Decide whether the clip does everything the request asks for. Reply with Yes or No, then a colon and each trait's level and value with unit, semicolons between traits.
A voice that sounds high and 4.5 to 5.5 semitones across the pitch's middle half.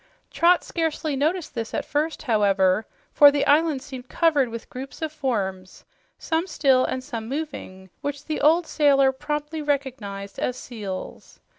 Yes: very high, 275 Hz; average, 5.1 semitones